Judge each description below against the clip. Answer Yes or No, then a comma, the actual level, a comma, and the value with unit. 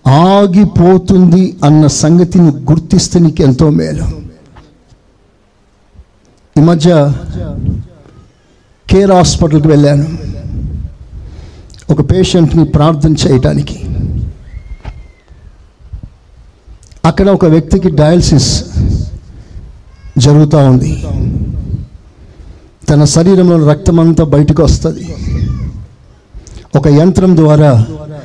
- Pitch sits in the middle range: Yes, medium, 150 Hz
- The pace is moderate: No, slow, 65 wpm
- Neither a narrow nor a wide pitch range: No, wide, 8.7 semitones